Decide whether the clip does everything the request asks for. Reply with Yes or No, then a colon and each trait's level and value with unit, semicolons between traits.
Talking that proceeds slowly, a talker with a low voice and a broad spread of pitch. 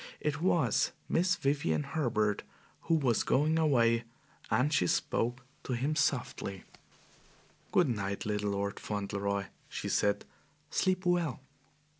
Yes: slow, 120 wpm; low, 125 Hz; wide, 7.0 semitones